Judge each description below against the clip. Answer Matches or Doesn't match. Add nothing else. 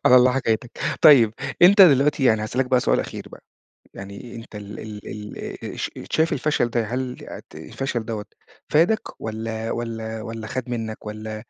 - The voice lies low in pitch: Matches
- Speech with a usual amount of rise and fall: Matches